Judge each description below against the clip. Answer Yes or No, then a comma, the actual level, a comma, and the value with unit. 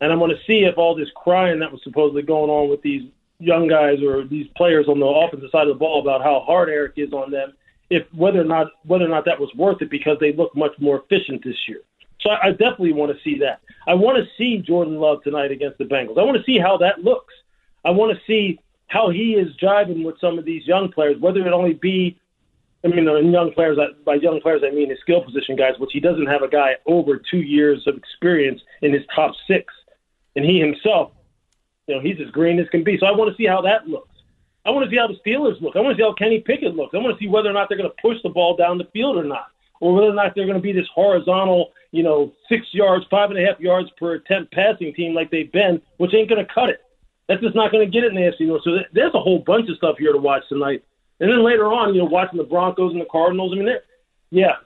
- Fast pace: Yes, fast, 270 wpm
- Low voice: No, medium, 175 Hz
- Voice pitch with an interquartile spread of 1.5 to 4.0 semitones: No, average, 4.7 semitones